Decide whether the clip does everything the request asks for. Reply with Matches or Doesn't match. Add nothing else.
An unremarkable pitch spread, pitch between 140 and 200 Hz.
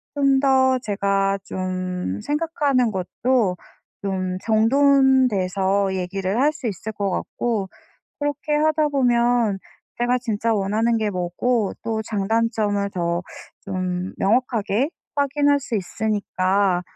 Doesn't match